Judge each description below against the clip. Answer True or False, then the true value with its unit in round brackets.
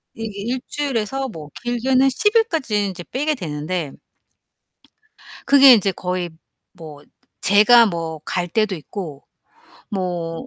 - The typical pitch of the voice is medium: False (205 Hz)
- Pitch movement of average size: False (6.8 semitones)